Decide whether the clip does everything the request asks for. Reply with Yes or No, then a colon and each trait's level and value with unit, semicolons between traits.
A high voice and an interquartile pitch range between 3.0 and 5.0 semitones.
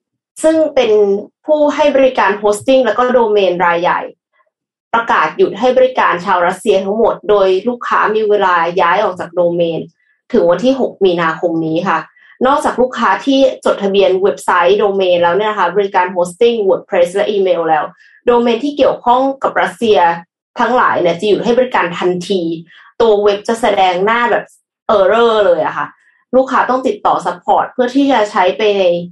No: high, 205 Hz; wide, 5.5 semitones